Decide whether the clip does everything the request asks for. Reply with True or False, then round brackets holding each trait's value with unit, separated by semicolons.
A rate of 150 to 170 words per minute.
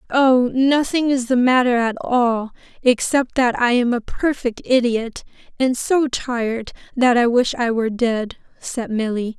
True (160 wpm)